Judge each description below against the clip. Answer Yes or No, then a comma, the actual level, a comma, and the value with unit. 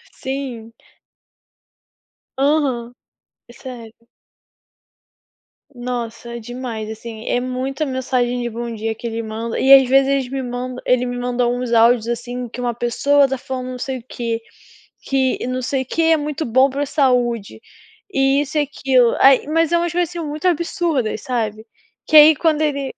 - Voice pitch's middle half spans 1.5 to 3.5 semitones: Yes, average, 2.7 semitones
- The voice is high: Yes, very high, 255 Hz